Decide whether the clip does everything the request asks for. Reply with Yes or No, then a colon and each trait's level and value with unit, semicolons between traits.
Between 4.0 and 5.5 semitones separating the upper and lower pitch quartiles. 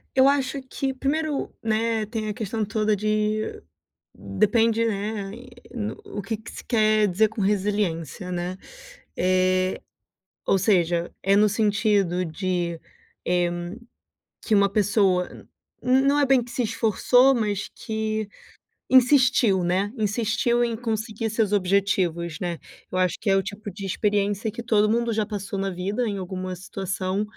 No: average, 3.1 semitones